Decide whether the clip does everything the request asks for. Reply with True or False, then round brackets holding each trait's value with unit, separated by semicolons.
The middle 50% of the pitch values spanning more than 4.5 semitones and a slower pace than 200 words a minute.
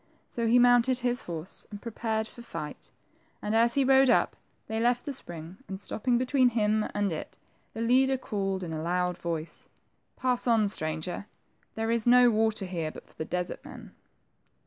True (5.2 semitones; 180 wpm)